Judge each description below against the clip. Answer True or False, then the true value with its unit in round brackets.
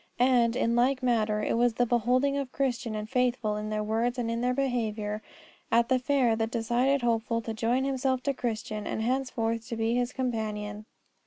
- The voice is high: True (235 Hz)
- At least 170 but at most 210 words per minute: True (190 wpm)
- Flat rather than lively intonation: True (2.3 semitones)